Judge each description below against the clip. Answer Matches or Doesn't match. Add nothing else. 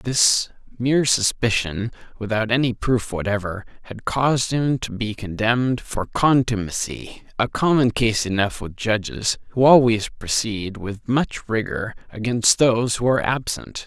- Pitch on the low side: Matches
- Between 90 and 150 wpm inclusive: Matches